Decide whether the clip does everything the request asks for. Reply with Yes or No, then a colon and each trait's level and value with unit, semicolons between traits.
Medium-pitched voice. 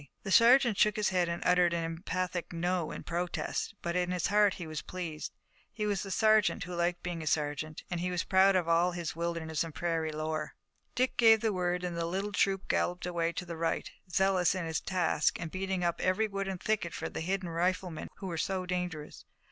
Yes: medium, 180 Hz